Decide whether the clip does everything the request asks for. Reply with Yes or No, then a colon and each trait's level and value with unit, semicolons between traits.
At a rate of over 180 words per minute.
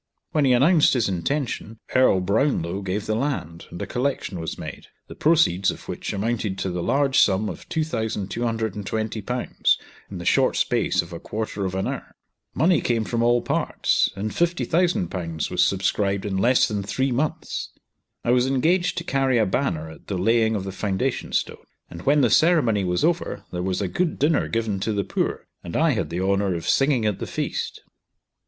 Yes: average, 190 wpm